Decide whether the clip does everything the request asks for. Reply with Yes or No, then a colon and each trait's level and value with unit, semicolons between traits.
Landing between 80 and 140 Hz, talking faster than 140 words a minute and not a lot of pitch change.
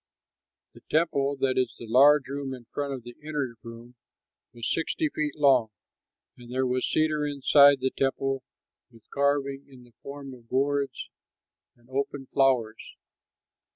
Yes: low, 135 Hz; average, 150 wpm; narrow, 2.3 semitones